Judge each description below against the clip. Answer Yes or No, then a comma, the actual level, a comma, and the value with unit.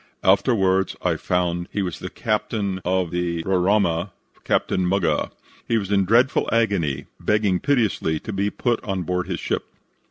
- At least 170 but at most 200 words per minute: No, average, 155 wpm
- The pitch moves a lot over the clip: No, average, 2.8 semitones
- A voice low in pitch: Yes, very low, 95 Hz